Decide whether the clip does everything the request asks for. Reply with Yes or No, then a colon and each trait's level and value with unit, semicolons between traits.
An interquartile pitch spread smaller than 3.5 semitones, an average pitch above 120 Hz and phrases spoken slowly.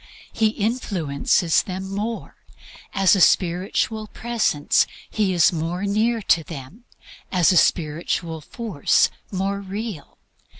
No: average, 4.3 semitones; high, 190 Hz; slow, 115 wpm